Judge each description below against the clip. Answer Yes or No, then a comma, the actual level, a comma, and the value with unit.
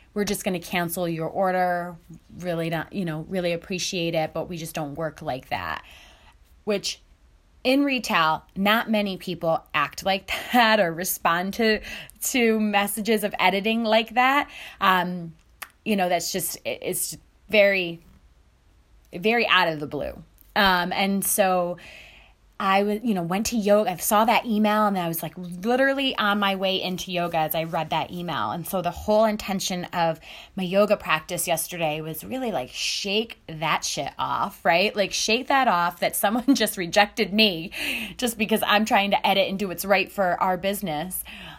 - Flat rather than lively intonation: No, average, 3.9 semitones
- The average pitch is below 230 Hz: Yes, medium, 185 Hz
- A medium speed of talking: Yes, average, 170 wpm